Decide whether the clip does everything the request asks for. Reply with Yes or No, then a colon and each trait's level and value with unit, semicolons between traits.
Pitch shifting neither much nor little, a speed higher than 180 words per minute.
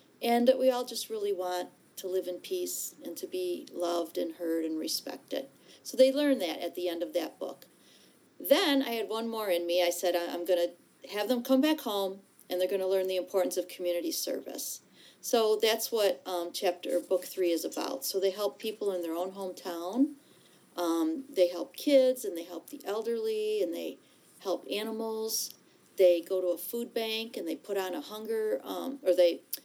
No: wide, 6.2 semitones; fast, 205 wpm